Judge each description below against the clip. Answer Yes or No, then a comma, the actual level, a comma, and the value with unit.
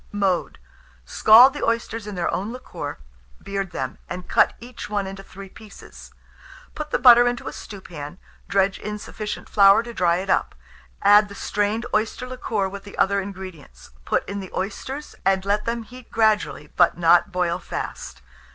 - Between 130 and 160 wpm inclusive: No, average, 170 wpm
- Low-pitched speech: No, high, 200 Hz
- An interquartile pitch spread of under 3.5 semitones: Yes, average, 2.9 semitones